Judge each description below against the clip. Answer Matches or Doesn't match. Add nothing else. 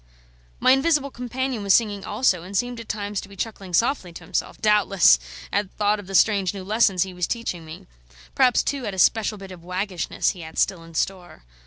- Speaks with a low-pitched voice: Doesn't match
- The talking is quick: Matches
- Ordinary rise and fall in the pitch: Matches